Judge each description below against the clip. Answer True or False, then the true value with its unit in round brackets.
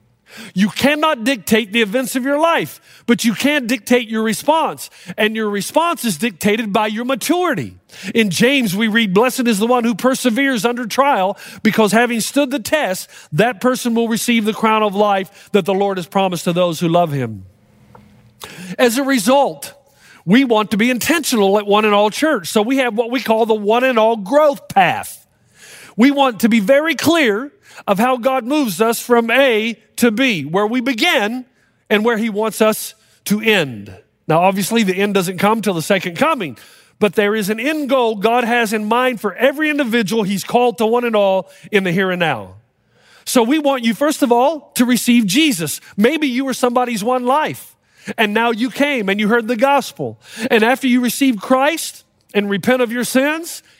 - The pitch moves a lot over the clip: False (4.2 semitones)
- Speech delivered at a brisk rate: False (195 wpm)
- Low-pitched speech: False (230 Hz)